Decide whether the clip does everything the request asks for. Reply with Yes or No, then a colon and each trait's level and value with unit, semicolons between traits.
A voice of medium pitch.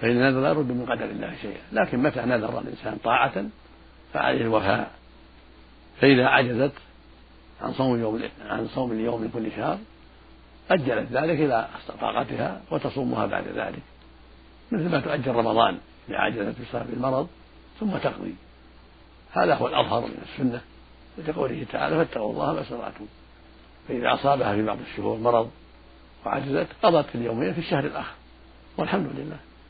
No: low, 100 Hz